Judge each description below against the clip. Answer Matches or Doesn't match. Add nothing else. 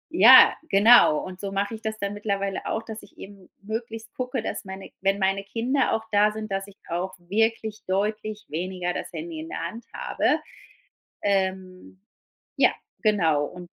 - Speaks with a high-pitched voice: Matches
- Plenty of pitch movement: Doesn't match